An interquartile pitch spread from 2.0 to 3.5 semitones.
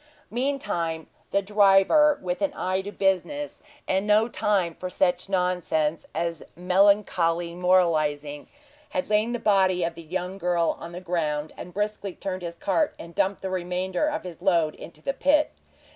Yes: average, 3.2 semitones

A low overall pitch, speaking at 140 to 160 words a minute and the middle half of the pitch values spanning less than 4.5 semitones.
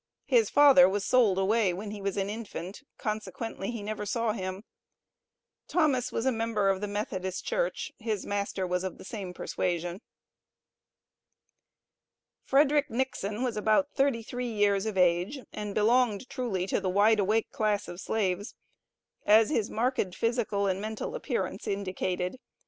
No: high, 210 Hz; average, 150 wpm; average, 3.4 semitones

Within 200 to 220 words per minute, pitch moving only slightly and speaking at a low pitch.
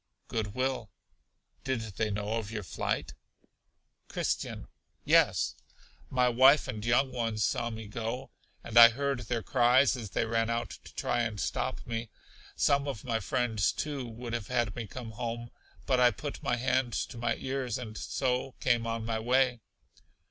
No: average, 170 wpm; narrow, 2.2 semitones; low, 120 Hz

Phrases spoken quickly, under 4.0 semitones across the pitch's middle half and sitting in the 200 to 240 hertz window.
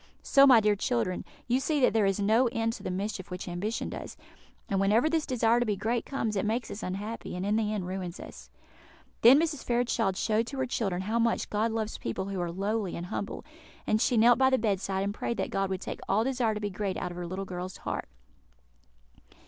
Yes: fast, 235 wpm; average, 3.5 semitones; high, 215 Hz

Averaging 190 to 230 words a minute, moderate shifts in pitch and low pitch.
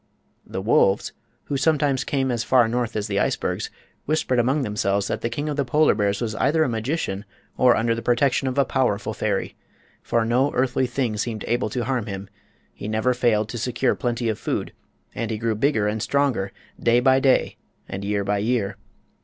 Yes: average, 195 wpm; average, 3.6 semitones; low, 120 Hz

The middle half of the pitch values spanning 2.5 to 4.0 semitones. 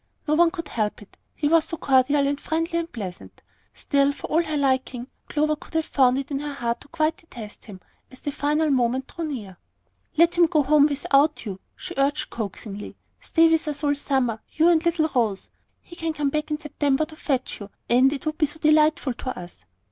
Yes: average, 3.4 semitones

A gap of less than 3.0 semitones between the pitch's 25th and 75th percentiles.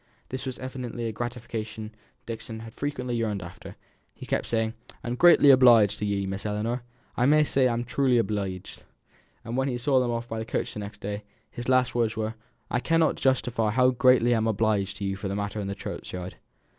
No: average, 3.3 semitones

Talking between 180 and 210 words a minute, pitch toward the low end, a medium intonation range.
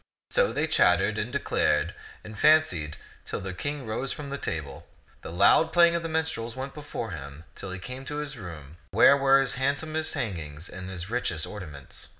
No: average, 185 wpm; low, 115 Hz; wide, 8.5 semitones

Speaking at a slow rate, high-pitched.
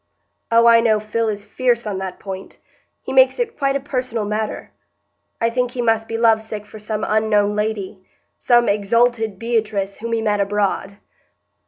No: average, 170 wpm; high, 220 Hz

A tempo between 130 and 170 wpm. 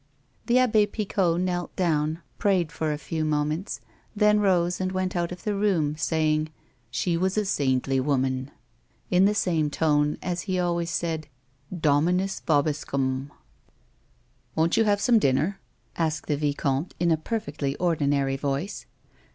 Yes: average, 160 wpm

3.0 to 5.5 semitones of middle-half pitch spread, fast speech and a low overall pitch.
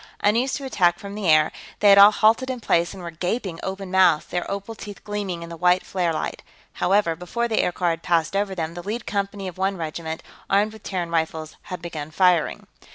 No: average, 3.3 semitones; fast, 220 wpm; medium, 185 Hz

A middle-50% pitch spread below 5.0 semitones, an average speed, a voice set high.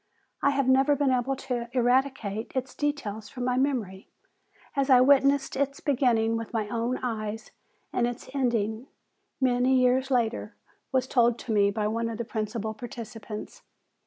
Yes: average, 3.0 semitones; average, 160 wpm; high, 245 Hz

